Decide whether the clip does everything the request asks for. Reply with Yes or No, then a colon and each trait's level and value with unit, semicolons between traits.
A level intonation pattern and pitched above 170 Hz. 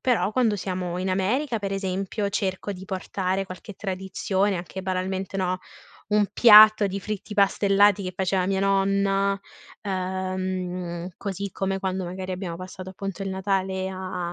Yes: narrow, 1.2 semitones; high, 190 Hz